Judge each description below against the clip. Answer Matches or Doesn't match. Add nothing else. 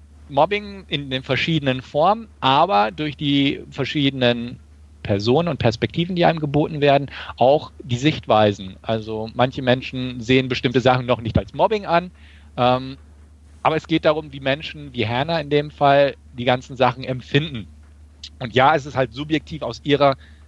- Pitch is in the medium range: Doesn't match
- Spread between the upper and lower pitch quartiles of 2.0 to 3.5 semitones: Doesn't match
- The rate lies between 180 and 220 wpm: Doesn't match